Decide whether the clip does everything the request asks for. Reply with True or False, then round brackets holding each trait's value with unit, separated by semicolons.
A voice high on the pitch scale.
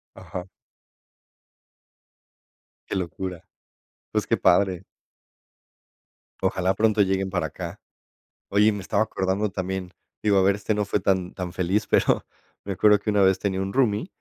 False (95 Hz)